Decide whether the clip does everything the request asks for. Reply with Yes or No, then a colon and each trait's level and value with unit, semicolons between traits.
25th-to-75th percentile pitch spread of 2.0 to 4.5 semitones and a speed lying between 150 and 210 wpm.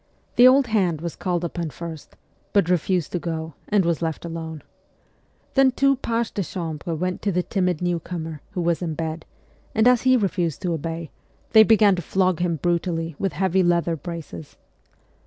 Yes: average, 2.9 semitones; average, 180 wpm